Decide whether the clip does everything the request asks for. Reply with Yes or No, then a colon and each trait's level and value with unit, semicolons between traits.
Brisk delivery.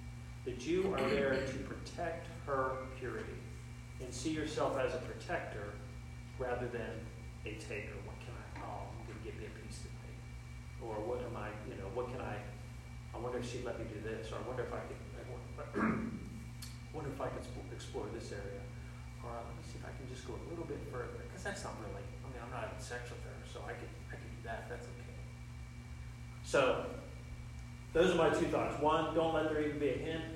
Yes: fast, 215 wpm